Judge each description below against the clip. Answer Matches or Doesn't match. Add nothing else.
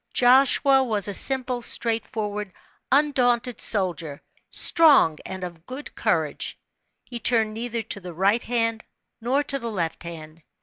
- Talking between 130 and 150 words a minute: Matches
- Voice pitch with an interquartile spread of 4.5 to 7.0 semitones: Matches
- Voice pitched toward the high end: Matches